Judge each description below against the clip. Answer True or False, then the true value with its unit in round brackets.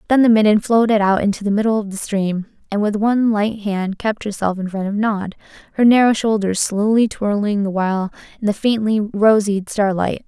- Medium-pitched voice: False (210 Hz)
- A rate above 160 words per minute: True (200 wpm)